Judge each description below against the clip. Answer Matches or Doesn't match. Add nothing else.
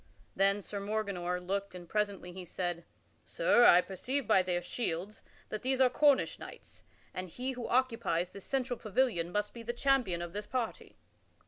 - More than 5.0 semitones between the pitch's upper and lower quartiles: Matches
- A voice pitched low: Doesn't match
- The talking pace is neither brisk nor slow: Matches